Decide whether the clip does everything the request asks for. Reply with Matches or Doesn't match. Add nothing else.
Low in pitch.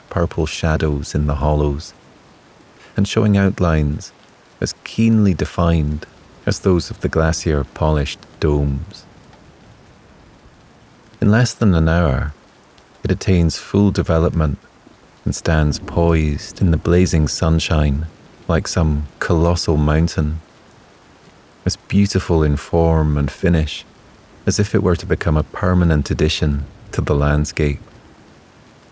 Matches